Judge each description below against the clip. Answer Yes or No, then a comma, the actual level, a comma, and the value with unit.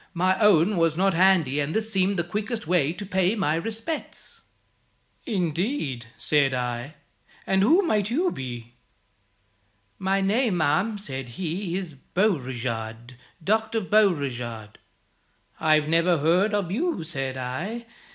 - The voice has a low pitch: No, medium, 175 Hz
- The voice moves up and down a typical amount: No, wide, 6.8 semitones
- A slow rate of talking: Yes, slow, 130 wpm